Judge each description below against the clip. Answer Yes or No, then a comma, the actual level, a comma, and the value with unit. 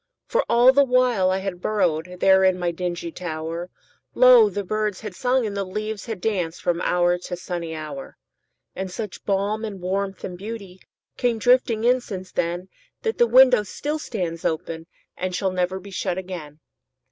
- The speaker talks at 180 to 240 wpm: No, average, 155 wpm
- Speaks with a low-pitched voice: No, high, 190 Hz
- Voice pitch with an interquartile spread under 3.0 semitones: No, average, 3.9 semitones